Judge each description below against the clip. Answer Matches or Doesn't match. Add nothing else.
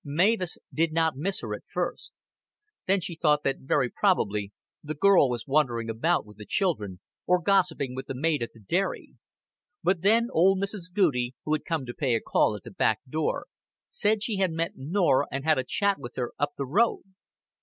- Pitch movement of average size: Doesn't match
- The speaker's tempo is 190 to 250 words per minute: Matches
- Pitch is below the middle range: Doesn't match